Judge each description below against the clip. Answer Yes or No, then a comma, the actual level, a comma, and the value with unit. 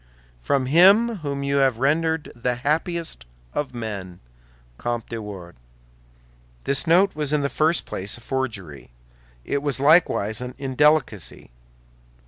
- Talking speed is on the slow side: Yes, slow, 130 wpm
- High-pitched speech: No, low, 135 Hz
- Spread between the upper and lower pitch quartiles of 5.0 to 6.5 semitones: Yes, average, 5.3 semitones